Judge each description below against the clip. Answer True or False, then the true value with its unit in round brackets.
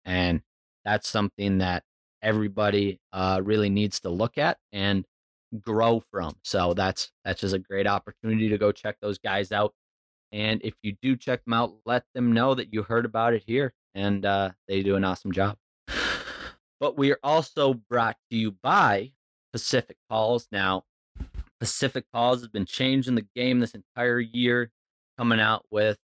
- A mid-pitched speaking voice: False (105 Hz)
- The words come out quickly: False (170 wpm)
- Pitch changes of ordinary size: True (3.4 semitones)